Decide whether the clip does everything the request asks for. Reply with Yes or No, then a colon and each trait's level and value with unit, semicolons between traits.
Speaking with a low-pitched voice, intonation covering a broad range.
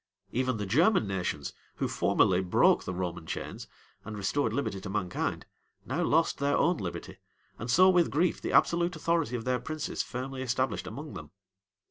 Yes: low, 125 Hz; wide, 8.4 semitones